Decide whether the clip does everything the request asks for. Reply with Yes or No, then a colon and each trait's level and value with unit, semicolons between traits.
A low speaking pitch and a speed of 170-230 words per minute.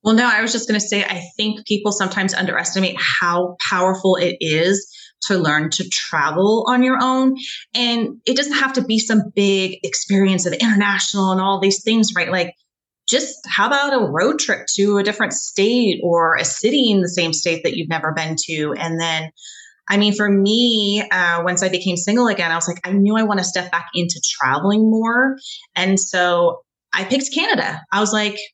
No: high, 200 Hz; average, 200 wpm